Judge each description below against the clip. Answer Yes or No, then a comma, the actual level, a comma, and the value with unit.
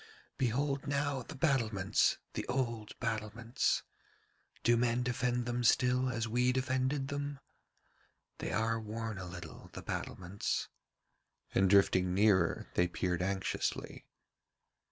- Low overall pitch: Yes, low, 115 Hz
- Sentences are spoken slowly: Yes, slow, 115 wpm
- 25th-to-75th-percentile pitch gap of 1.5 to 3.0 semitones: No, average, 4.1 semitones